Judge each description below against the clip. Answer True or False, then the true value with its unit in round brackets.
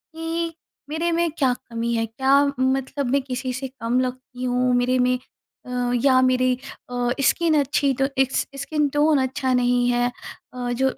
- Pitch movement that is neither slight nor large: False (2.2 semitones)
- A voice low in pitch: False (255 Hz)